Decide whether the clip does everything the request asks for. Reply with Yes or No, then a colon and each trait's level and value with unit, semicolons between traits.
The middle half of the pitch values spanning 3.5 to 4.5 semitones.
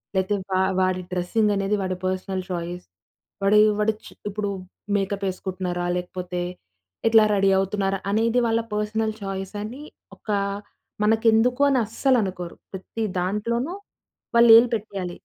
No: average, 3.0 semitones